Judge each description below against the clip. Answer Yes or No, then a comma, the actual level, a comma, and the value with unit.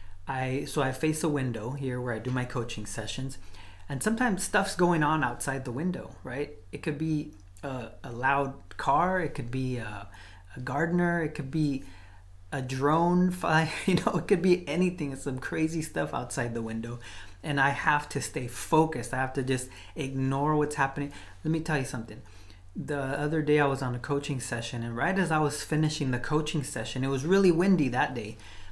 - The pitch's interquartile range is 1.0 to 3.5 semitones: No, average, 4.6 semitones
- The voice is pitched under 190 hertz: Yes, low, 135 Hz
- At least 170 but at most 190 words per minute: No, average, 200 wpm